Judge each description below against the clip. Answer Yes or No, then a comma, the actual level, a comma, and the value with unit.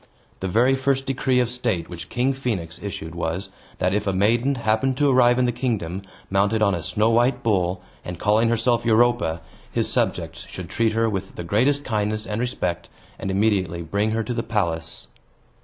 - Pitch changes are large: No, average, 4.7 semitones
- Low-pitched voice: Yes, low, 110 Hz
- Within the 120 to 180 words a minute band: No, average, 190 wpm